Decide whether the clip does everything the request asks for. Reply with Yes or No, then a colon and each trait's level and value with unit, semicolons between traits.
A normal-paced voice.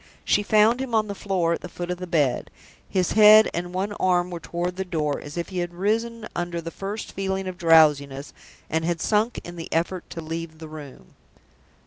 No: fast, 210 wpm